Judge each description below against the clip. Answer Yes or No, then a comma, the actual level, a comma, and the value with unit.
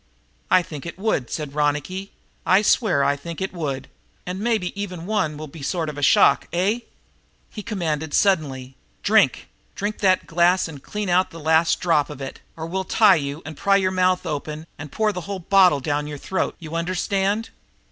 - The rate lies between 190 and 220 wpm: Yes, average, 195 wpm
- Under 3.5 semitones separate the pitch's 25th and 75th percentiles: No, average, 4.3 semitones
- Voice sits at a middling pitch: Yes, medium, 170 Hz